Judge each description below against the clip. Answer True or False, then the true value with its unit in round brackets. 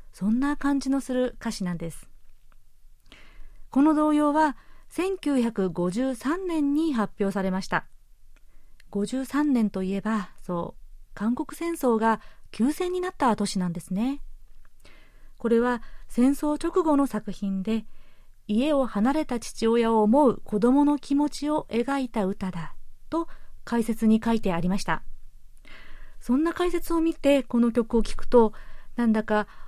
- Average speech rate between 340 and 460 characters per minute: False (245 characters per minute)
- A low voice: False (235 Hz)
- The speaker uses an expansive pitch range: True (5.9 semitones)